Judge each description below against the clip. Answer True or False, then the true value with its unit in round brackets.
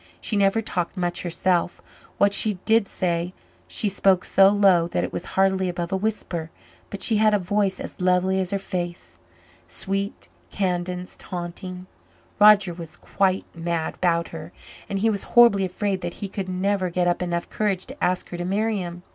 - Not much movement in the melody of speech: True (2.3 semitones)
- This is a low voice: False (185 Hz)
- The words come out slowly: False (180 wpm)